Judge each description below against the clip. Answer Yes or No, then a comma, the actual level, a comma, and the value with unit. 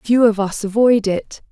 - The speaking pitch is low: No, high, 215 Hz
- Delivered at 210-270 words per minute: No, average, 200 wpm